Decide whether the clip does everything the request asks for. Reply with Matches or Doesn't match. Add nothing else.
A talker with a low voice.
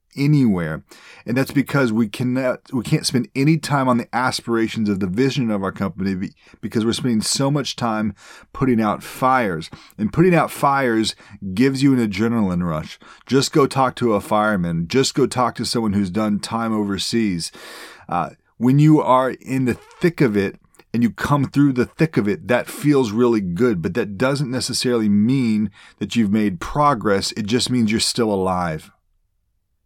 Matches